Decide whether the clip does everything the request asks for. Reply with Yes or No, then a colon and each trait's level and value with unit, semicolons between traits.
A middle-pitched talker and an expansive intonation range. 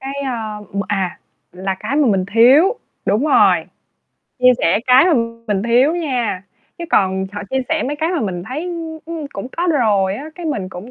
No: very high, 250 Hz; wide, 7.4 semitones